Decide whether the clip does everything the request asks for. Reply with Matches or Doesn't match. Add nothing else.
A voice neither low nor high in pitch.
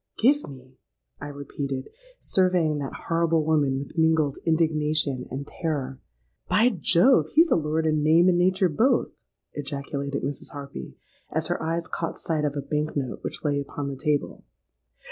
Matches